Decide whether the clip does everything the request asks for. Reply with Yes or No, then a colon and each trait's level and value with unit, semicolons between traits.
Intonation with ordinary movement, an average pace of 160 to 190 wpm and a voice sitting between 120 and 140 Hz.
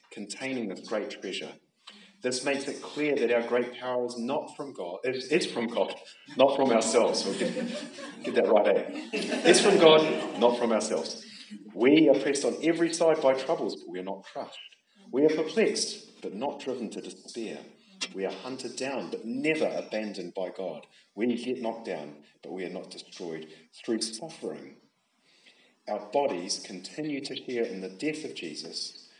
No: wide, 6.4 semitones; average, 175 wpm; low, 135 Hz